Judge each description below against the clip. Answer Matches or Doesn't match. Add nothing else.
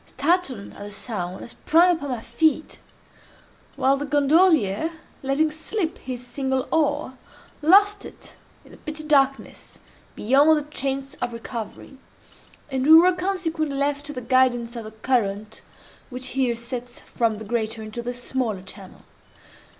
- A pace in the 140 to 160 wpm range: Matches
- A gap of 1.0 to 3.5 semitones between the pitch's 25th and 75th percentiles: Doesn't match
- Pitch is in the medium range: Doesn't match